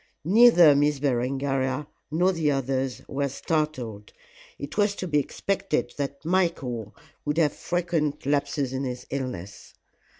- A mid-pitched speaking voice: Yes, medium, 145 Hz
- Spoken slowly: Yes, slow, 130 wpm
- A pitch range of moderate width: Yes, average, 3.6 semitones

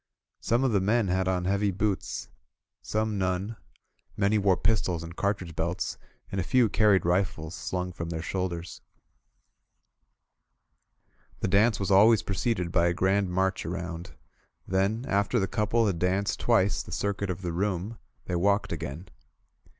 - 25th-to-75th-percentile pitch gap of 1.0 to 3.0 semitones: Yes, narrow, 2.5 semitones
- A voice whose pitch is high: No, very low, 95 Hz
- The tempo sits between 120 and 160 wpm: Yes, average, 155 wpm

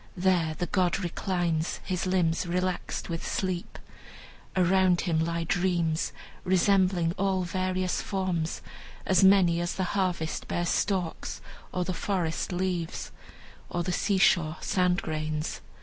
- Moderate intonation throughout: No, narrow, 1.8 semitones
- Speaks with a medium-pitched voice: Yes, medium, 180 Hz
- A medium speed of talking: No, slow, 125 wpm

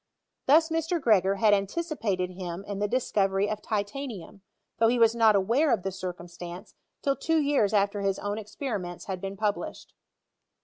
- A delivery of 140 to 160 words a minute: No, average, 170 wpm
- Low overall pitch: No, high, 205 Hz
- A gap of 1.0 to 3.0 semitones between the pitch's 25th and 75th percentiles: No, average, 3.8 semitones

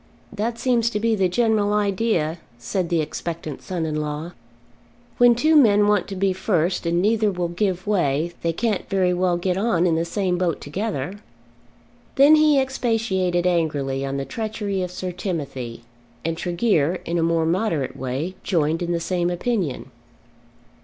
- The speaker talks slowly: No, average, 165 wpm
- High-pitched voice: No, medium, 180 Hz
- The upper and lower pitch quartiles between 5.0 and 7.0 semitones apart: No, average, 4.1 semitones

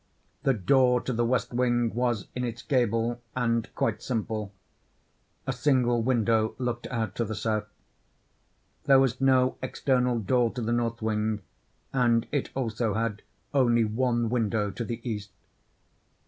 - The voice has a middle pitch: No, low, 120 Hz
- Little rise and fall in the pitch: Yes, narrow, 2.2 semitones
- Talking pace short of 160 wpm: Yes, average, 145 wpm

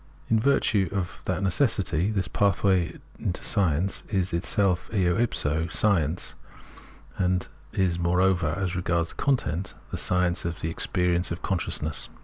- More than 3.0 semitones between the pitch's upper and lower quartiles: No, narrow, 2.4 semitones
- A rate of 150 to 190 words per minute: No, slow, 135 wpm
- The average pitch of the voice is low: Yes, very low, 90 Hz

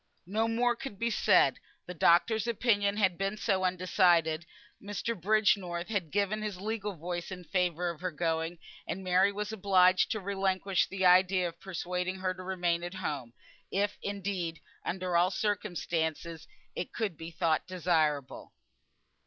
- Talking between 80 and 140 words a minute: No, average, 155 wpm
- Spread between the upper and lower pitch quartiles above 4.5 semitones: No, average, 2.7 semitones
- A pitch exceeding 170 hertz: Yes, medium, 185 Hz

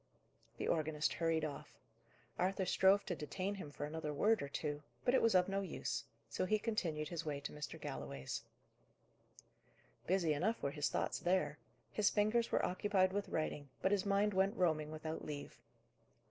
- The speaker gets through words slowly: No, average, 175 wpm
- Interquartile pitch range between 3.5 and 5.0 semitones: Yes, average, 4.7 semitones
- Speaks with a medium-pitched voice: Yes, medium, 175 Hz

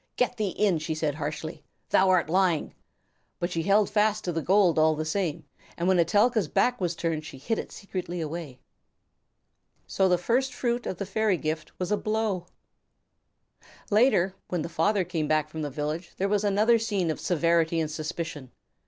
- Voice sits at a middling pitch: Yes, medium, 175 Hz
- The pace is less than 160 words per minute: No, average, 185 wpm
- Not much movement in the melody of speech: No, average, 4.4 semitones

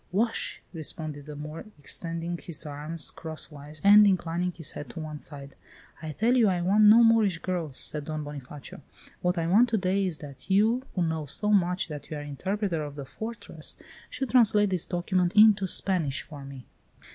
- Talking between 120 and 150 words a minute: No, average, 185 wpm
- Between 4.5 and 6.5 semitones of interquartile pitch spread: Yes, average, 5.1 semitones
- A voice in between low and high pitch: Yes, medium, 170 Hz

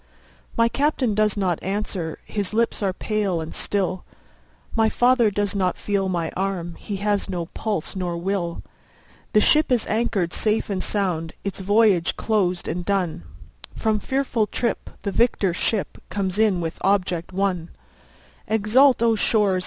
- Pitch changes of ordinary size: Yes, average, 3.1 semitones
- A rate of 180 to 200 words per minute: No, average, 155 wpm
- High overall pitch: Yes, high, 200 Hz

